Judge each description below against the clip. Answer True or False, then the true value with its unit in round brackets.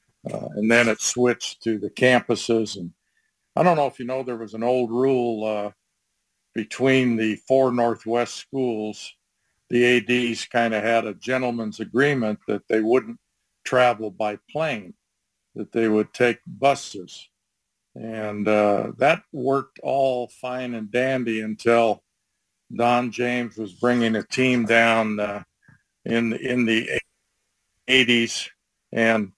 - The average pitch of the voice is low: True (115 Hz)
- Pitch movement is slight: True (2.3 semitones)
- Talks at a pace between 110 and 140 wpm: True (135 wpm)